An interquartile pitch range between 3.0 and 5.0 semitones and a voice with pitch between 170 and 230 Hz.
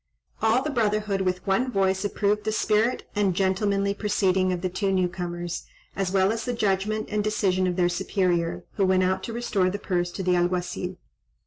No: narrow, 2.4 semitones; high, 190 Hz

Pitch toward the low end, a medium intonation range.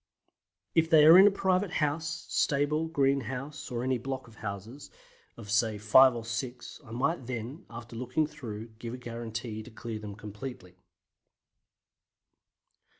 Yes: low, 125 Hz; average, 4.3 semitones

